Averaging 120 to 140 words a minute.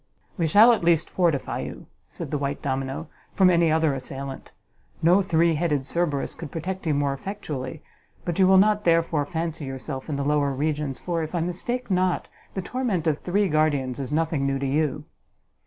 No: average, 190 wpm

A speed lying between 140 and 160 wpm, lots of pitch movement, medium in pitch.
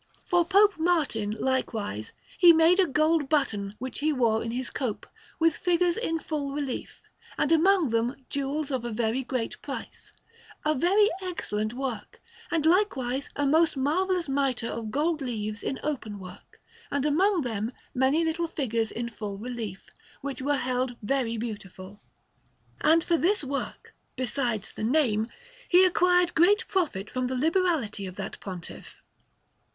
No: average, 150 wpm; wide, 6.3 semitones; very high, 275 Hz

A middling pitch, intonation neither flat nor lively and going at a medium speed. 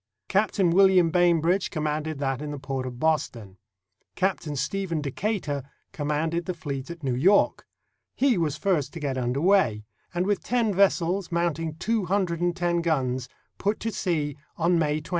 Yes: medium, 165 Hz; average, 4.2 semitones; average, 170 wpm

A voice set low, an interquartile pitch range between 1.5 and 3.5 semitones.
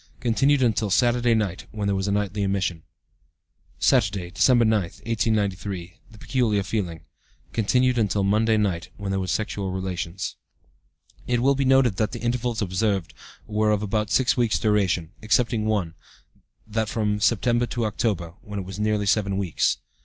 Yes: low, 105 Hz; average, 2.9 semitones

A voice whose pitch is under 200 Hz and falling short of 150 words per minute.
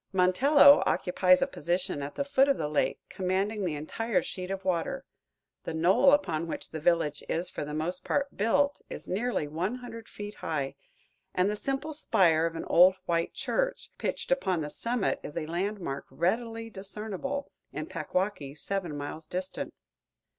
No: medium, 185 Hz; average, 170 wpm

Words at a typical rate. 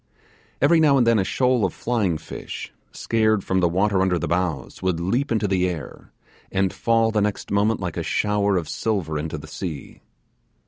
Yes: average, 190 wpm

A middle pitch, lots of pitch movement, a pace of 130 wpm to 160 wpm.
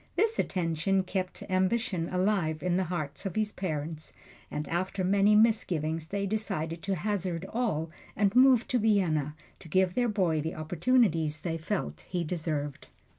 No: medium, 180 Hz; average, 4.4 semitones; average, 155 wpm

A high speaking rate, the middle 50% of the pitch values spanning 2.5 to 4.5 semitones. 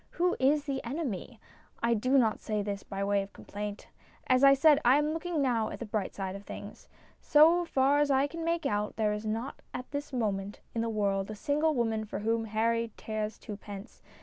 No: fast, 210 wpm; average, 5.2 semitones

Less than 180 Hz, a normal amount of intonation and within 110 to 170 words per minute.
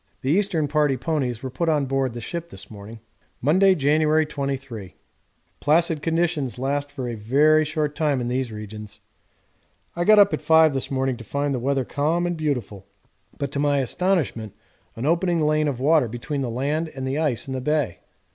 No: medium, 140 Hz; average, 3.6 semitones; average, 190 wpm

